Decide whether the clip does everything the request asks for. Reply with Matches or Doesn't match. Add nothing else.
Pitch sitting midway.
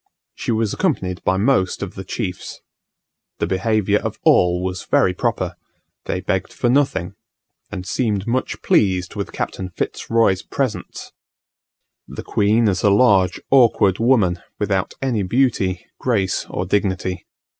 Doesn't match